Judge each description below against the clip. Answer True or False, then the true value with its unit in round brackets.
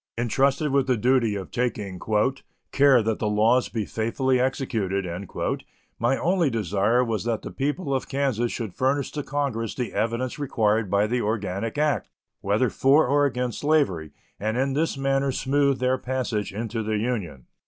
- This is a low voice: True (125 Hz)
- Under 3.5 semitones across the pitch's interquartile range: False (4.1 semitones)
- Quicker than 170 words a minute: False (165 wpm)